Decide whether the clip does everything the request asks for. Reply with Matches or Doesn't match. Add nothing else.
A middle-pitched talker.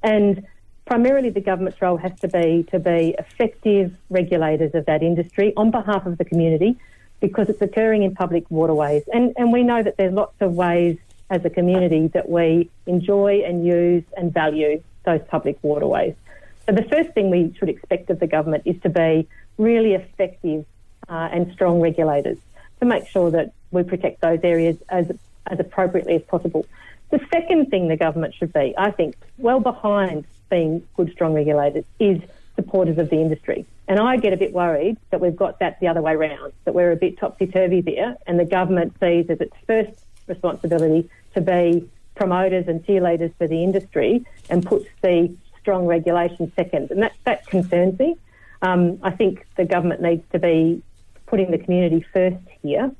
Matches